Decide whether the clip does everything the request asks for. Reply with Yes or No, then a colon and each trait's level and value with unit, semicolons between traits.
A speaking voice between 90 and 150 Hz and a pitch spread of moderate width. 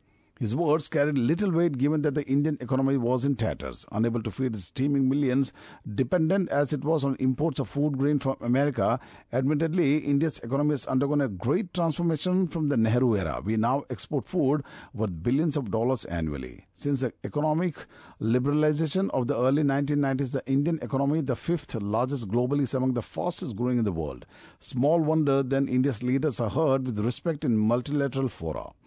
Yes: low, 135 Hz; average, 3.5 semitones